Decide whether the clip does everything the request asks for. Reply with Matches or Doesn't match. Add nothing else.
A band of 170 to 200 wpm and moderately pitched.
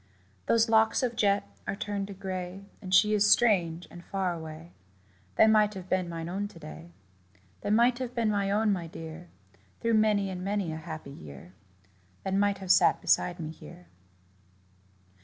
Doesn't match